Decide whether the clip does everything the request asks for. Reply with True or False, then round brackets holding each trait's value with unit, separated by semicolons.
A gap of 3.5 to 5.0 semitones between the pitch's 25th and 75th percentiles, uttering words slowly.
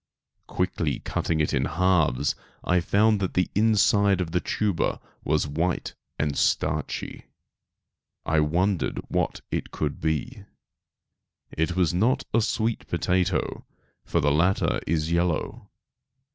True (3.9 semitones; 125 wpm)